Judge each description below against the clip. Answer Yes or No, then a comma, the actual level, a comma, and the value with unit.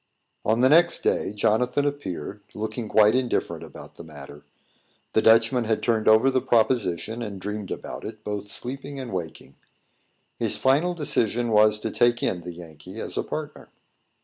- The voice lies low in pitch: Yes, low, 110 Hz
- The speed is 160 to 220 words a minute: Yes, average, 165 wpm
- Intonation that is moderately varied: Yes, average, 3.5 semitones